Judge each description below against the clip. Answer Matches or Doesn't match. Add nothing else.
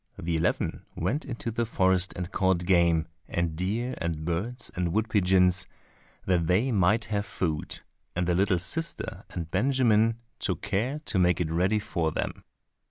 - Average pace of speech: Matches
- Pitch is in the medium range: Doesn't match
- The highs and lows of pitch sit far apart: Doesn't match